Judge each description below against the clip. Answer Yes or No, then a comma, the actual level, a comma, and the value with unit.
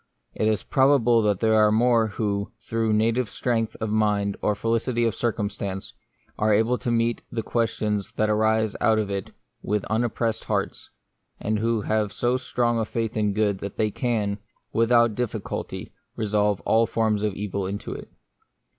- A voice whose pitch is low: Yes, low, 110 Hz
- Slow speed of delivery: No, average, 165 wpm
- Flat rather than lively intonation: Yes, narrow, 1.7 semitones